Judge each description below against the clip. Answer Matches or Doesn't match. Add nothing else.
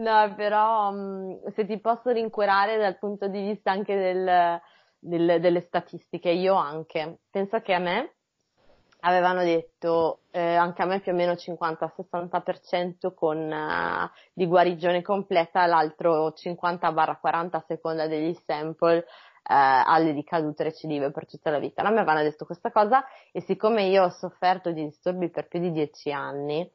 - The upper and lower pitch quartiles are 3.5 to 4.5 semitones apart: Doesn't match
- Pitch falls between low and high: Matches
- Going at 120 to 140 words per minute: Doesn't match